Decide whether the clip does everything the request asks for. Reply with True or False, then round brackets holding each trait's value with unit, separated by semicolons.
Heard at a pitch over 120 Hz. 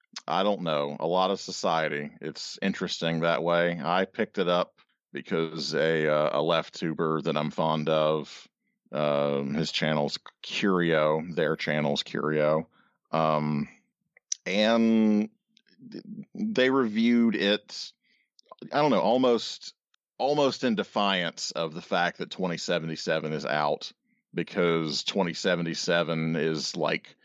False (80 Hz)